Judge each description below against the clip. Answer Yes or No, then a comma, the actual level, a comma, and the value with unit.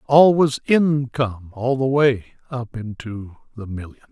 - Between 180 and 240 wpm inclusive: No, average, 145 wpm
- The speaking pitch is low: Yes, low, 125 Hz